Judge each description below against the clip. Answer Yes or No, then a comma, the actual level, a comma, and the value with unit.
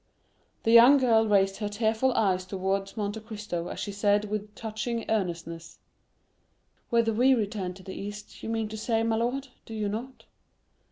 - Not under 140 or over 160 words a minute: No, average, 170 wpm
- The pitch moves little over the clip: Yes, narrow, 2.2 semitones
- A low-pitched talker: No, high, 215 Hz